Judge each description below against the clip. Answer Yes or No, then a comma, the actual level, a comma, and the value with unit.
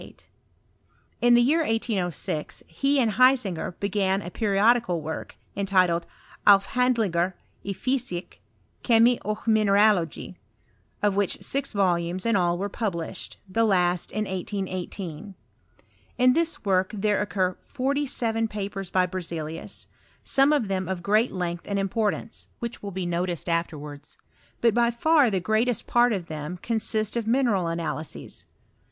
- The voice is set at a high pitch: Yes, high, 200 Hz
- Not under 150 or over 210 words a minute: No, average, 140 wpm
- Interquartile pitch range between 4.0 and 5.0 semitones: Yes, average, 4.4 semitones